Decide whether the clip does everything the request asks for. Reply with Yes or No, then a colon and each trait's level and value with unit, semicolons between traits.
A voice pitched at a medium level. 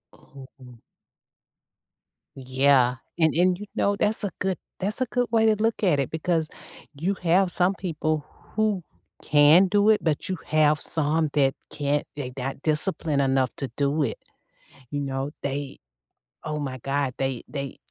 Yes: medium, 150 Hz